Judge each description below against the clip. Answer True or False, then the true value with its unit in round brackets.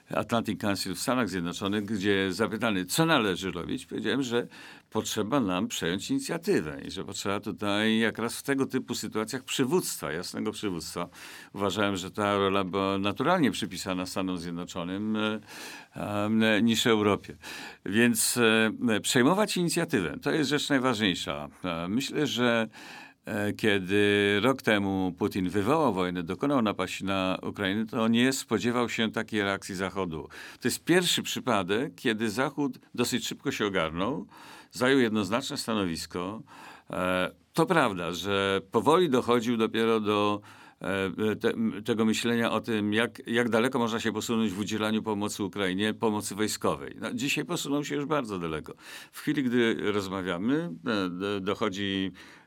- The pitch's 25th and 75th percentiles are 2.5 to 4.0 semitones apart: True (3.3 semitones)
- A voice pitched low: True (110 Hz)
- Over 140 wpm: False (130 wpm)